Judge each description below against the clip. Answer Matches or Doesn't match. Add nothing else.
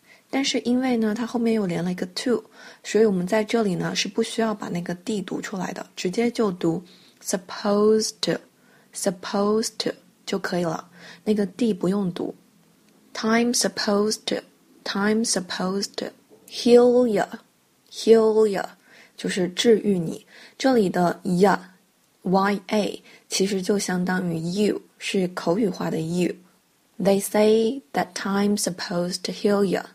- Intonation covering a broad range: Doesn't match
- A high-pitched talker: Matches